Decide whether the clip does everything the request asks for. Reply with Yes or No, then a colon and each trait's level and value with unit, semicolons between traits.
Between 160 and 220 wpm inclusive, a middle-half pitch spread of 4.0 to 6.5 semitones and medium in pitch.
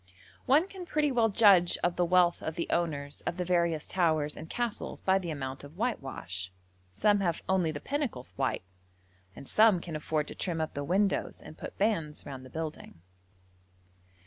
Yes: average, 180 wpm; average, 5.0 semitones; medium, 170 Hz